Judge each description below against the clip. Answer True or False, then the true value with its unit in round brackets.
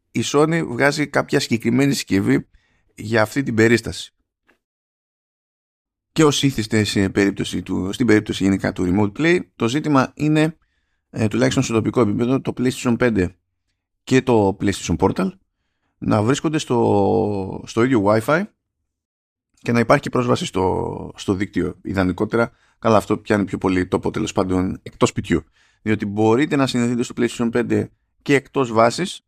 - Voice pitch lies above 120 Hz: False (110 Hz)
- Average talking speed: True (150 wpm)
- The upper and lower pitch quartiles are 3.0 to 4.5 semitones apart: False (5.1 semitones)